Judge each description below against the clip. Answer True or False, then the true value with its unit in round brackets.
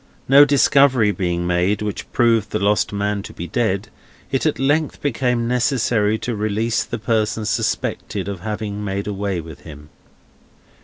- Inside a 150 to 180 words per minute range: True (155 wpm)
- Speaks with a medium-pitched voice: False (105 Hz)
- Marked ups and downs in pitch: False (3.1 semitones)